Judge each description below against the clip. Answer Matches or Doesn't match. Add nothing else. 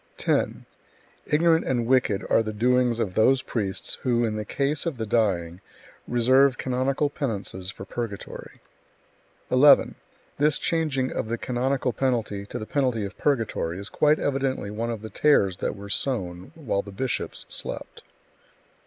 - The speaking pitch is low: Matches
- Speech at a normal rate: Matches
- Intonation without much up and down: Doesn't match